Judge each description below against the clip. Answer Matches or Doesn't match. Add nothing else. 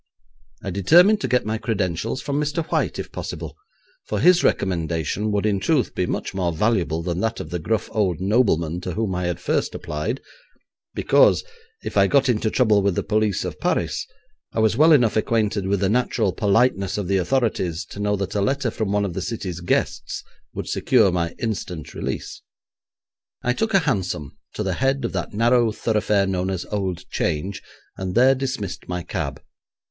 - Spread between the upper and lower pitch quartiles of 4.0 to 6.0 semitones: Matches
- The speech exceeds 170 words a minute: Matches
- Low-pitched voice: Matches